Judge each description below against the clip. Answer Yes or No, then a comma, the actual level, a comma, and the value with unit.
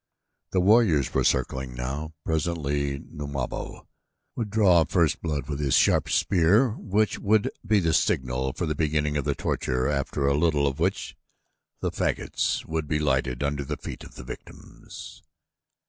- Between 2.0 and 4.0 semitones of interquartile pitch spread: Yes, average, 3.7 semitones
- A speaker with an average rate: Yes, average, 160 wpm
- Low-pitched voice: Yes, very low, 75 Hz